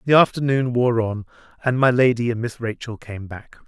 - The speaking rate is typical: Yes, average, 195 wpm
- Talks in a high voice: No, low, 120 Hz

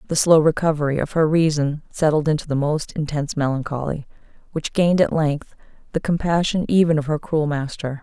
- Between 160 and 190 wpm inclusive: Yes, average, 170 wpm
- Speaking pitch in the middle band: Yes, medium, 155 Hz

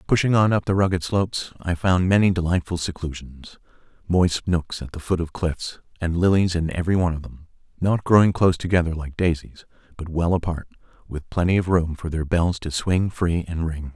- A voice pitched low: Yes, very low, 85 Hz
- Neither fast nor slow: Yes, average, 195 wpm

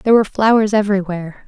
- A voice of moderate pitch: No, high, 205 Hz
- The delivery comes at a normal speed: Yes, average, 165 wpm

